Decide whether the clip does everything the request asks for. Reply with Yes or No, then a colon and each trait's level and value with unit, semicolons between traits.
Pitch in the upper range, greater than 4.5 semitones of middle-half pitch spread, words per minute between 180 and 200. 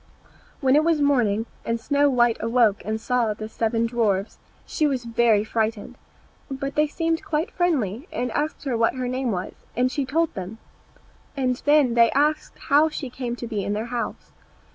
No: high, 245 Hz; average, 4.2 semitones; average, 185 wpm